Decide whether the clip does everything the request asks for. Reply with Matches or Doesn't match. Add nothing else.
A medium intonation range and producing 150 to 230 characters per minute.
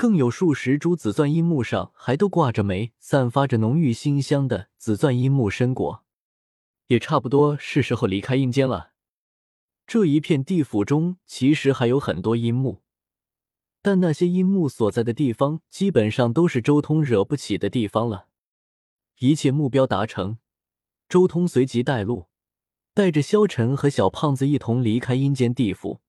Doesn't match